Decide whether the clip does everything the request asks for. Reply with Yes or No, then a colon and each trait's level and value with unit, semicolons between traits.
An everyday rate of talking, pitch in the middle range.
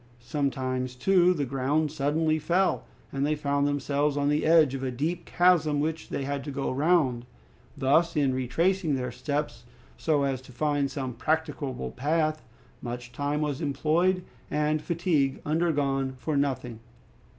Yes: average, 150 wpm; medium, 145 Hz